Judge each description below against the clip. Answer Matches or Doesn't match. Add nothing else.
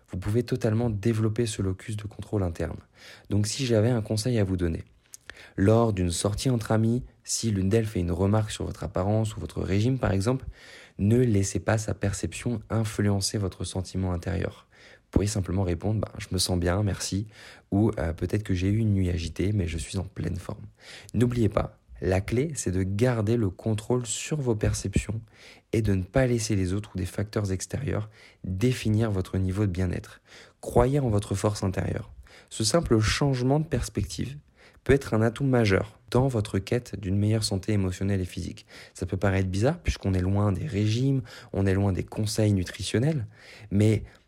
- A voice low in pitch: Matches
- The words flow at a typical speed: Matches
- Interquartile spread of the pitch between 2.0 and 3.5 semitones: Matches